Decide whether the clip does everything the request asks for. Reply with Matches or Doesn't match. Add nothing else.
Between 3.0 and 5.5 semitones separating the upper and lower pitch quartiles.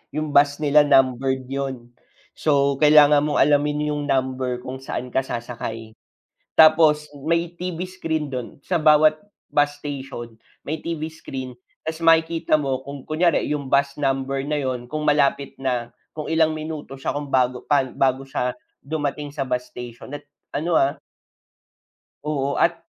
Doesn't match